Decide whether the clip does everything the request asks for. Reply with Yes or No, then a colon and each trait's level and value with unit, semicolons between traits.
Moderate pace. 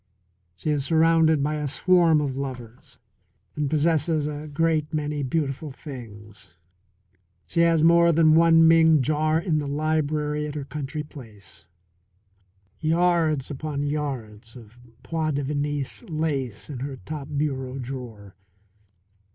No: slow, 125 wpm